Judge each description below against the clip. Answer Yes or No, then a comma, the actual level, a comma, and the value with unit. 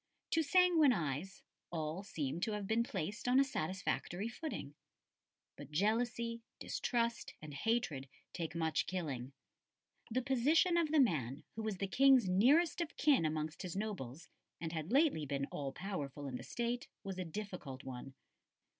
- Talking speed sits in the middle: Yes, average, 155 wpm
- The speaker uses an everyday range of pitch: No, wide, 7.9 semitones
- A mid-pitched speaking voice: No, high, 195 Hz